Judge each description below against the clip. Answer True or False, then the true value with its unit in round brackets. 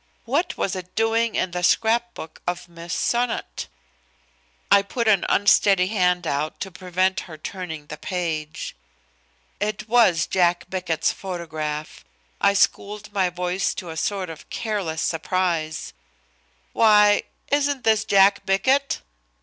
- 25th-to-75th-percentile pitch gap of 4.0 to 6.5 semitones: False (3.6 semitones)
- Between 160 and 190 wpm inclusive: False (135 wpm)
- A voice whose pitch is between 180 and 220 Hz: True (185 Hz)